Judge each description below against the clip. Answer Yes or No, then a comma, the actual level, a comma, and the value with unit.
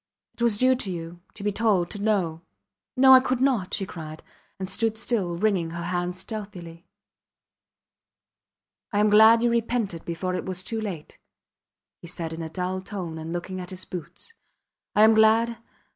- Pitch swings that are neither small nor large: Yes, average, 4.1 semitones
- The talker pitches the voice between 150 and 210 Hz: Yes, high, 190 Hz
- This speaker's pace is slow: No, average, 175 wpm